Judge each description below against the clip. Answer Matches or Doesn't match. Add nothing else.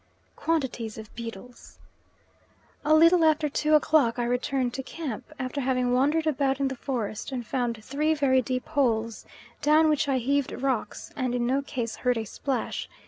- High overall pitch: Matches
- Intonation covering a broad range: Doesn't match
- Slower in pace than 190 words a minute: Matches